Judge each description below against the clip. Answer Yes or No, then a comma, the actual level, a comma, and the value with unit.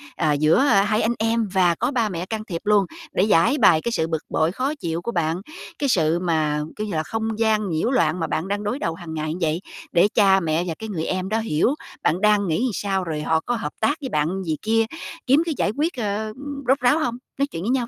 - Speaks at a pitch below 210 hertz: Yes, high, 195 Hz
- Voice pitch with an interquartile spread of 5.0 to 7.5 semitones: Yes, wide, 5.5 semitones